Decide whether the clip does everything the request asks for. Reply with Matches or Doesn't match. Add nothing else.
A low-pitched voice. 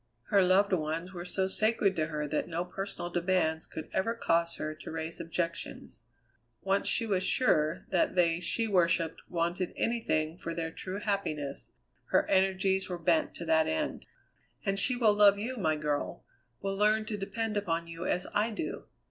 Doesn't match